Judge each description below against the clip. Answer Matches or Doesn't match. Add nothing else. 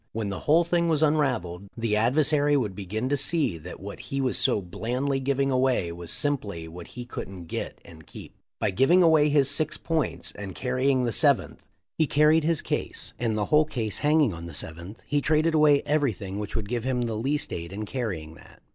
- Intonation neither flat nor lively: Doesn't match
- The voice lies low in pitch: Matches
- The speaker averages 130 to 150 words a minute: Doesn't match